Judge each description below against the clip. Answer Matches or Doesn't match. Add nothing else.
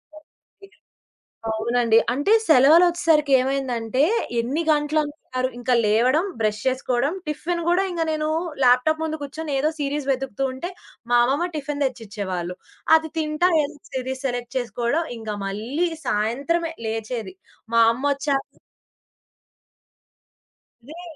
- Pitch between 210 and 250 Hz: Doesn't match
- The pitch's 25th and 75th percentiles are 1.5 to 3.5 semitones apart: Doesn't match